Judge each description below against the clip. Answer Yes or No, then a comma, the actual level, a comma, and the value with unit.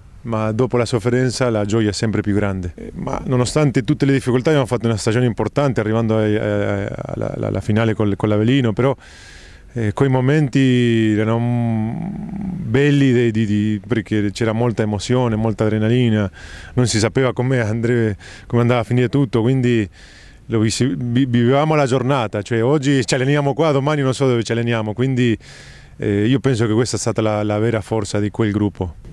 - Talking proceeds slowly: No, average, 165 wpm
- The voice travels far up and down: No, average, 3.3 semitones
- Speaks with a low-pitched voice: Yes, low, 115 Hz